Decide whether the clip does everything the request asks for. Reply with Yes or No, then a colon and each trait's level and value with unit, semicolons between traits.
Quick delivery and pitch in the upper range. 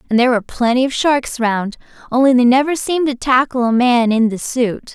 Yes: fast, 220 wpm; very high, 250 Hz